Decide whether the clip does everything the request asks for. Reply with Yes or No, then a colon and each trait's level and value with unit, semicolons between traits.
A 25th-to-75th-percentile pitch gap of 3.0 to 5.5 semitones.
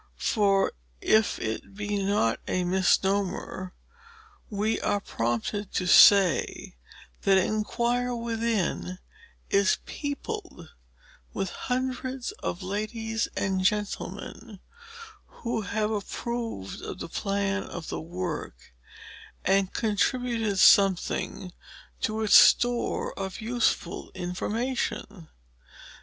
Yes: average, 3.3 semitones